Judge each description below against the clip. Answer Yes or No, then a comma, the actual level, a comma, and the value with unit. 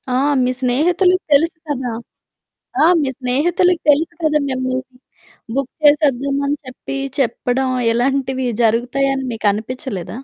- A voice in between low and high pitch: No, very high, 265 Hz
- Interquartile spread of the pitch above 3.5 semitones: No, average, 2.8 semitones